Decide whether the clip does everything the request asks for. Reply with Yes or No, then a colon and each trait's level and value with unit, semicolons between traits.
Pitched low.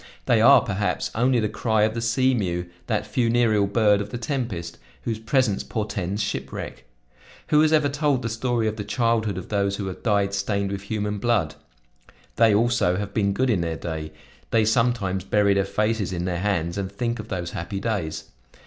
Yes: low, 105 Hz